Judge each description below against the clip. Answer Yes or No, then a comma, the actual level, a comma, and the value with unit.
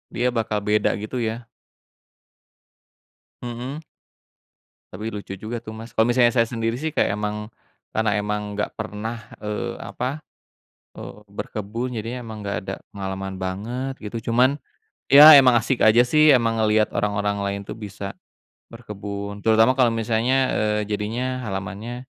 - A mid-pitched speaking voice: No, low, 110 Hz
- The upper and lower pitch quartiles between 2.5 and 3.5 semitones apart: Yes, average, 2.8 semitones